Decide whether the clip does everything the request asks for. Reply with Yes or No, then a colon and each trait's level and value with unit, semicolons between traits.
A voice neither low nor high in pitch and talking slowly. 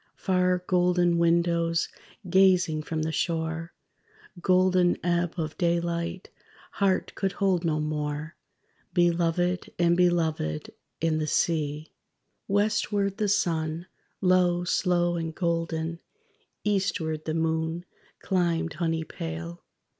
Yes: medium, 170 Hz; slow, 105 wpm